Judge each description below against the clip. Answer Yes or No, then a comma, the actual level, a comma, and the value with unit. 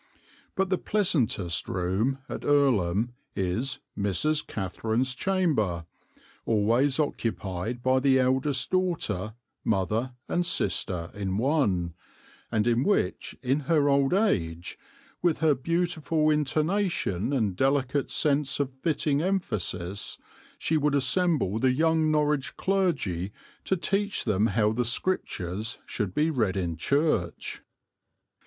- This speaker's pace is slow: Yes, slow, 120 wpm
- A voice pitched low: Yes, low, 130 Hz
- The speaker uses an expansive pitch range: Yes, wide, 7.2 semitones